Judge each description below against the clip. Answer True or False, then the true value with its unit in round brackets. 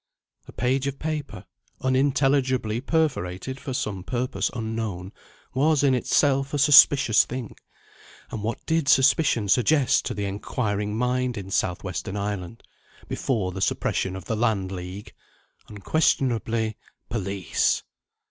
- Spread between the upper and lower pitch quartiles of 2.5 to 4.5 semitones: False (5.1 semitones)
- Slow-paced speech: True (125 wpm)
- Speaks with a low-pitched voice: True (115 Hz)